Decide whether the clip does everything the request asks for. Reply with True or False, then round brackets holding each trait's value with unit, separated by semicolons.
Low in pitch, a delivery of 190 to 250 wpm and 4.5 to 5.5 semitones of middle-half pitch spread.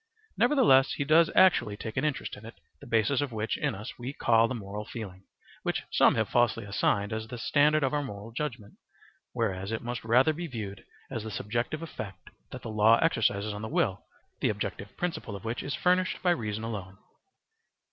True (115 Hz; 200 wpm; 5.0 semitones)